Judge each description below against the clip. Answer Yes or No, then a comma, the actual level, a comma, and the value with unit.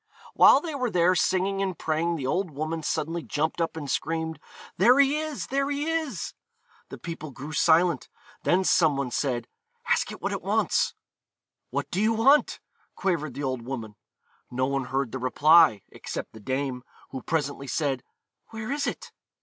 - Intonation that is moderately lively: No, wide, 6.0 semitones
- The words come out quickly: No, average, 175 wpm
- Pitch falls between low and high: Yes, medium, 160 Hz